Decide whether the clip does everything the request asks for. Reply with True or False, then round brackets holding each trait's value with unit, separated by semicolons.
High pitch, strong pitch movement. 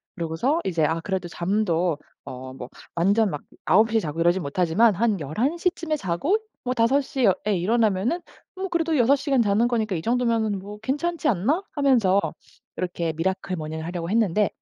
True (205 Hz; 6.4 semitones)